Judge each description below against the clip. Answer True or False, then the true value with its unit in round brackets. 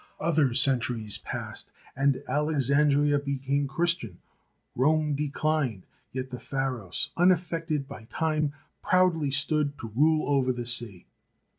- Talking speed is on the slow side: True (115 wpm)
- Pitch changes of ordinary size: True (3.2 semitones)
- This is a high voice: False (140 Hz)